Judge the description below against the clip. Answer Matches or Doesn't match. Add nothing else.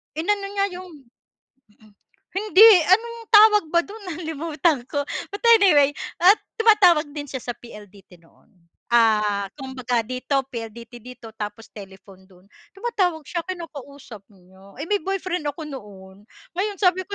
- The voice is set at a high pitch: Matches